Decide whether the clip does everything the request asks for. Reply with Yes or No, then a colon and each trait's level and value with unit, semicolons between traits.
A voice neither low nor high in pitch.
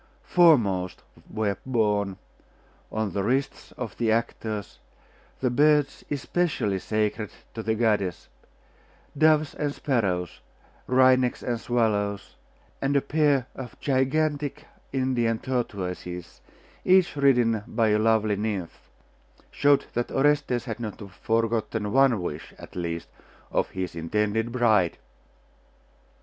No: low, 115 Hz